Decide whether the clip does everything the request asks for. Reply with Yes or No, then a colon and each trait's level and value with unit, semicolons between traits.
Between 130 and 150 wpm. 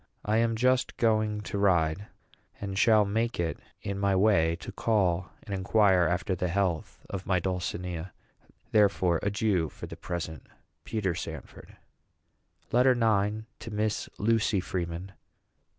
Yes: slow, 135 wpm